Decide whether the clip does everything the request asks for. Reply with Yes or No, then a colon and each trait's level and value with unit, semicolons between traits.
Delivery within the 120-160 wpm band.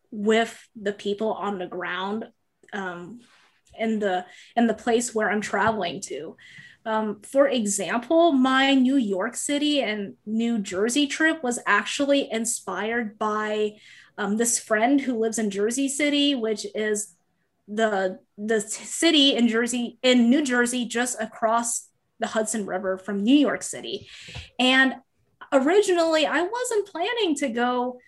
Yes: average, 140 wpm